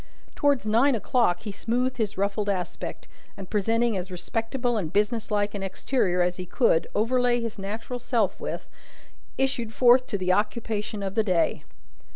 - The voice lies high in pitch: Yes, high, 215 Hz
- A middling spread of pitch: Yes, average, 3.5 semitones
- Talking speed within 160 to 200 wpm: Yes, average, 165 wpm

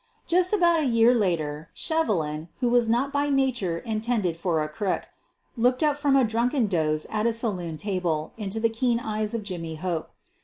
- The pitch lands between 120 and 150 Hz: No, high, 220 Hz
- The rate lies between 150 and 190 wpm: Yes, average, 185 wpm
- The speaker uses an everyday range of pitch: No, wide, 6.4 semitones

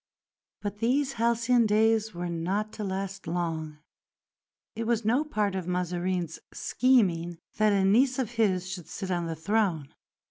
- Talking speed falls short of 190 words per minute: Yes, average, 150 wpm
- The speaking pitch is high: Yes, high, 200 Hz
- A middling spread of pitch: Yes, average, 4.3 semitones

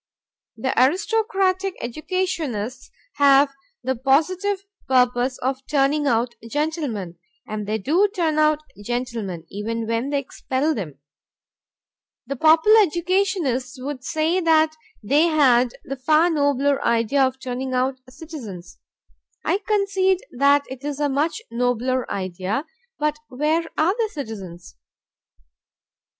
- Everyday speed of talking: No, slow, 120 wpm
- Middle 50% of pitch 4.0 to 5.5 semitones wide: Yes, average, 4.7 semitones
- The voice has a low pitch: No, very high, 275 Hz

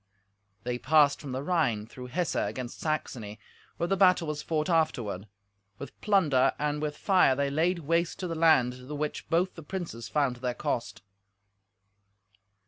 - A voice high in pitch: No, medium, 150 Hz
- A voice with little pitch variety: No, average, 4.8 semitones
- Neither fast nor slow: Yes, average, 165 wpm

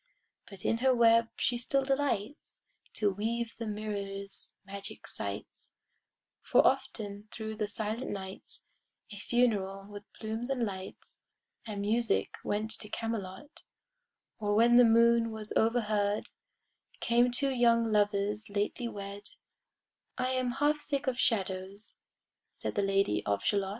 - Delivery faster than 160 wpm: No, slow, 135 wpm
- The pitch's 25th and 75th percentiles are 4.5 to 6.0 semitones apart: No, average, 2.8 semitones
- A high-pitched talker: Yes, high, 220 Hz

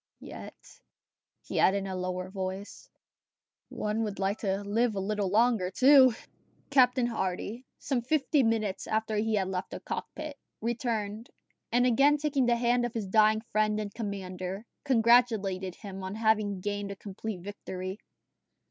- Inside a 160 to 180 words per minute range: No, average, 150 wpm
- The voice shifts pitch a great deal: No, average, 3.6 semitones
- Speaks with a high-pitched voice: Yes, high, 215 Hz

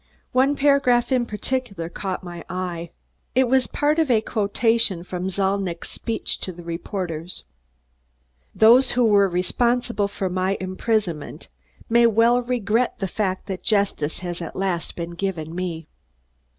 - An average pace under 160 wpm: Yes, average, 140 wpm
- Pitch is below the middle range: No, high, 200 Hz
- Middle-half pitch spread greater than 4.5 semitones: Yes, average, 5.0 semitones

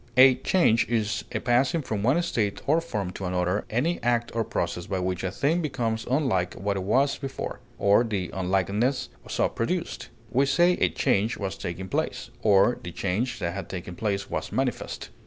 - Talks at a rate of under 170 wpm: No, average, 185 wpm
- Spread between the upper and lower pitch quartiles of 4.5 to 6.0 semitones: Yes, wide, 5.5 semitones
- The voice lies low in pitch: Yes, low, 110 Hz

